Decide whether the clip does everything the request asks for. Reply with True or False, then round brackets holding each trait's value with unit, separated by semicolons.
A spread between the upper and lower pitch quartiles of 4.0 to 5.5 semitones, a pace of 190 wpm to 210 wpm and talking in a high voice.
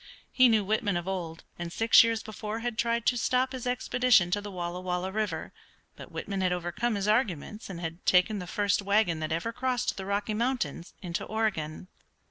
True (4.4 semitones; 195 wpm; 205 Hz)